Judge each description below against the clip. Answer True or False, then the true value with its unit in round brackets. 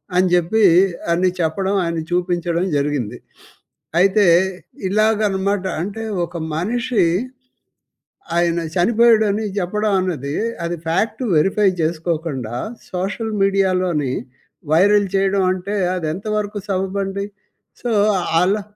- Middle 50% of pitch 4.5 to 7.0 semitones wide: False (3.3 semitones)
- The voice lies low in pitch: False (190 Hz)